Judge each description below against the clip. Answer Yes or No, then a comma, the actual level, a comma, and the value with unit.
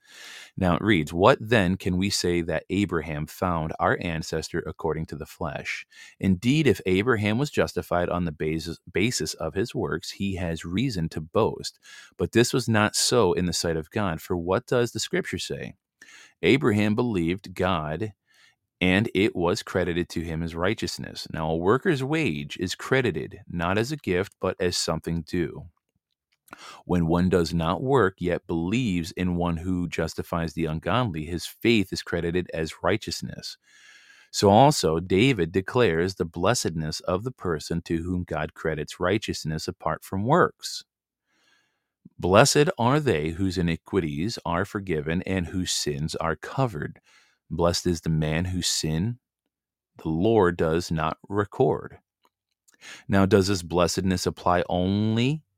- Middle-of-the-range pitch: No, very low, 90 Hz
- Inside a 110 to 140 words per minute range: No, average, 150 wpm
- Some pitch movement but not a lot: Yes, average, 3.4 semitones